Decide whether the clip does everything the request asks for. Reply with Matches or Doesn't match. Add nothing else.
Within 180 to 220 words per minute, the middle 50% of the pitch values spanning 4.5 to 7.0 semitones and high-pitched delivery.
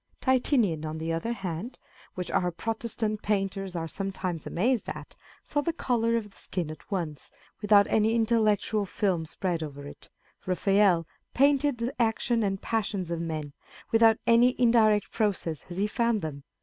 Doesn't match